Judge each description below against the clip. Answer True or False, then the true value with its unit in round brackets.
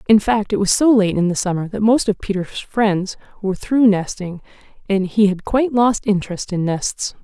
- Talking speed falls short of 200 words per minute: False (205 wpm)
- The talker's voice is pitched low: False (205 Hz)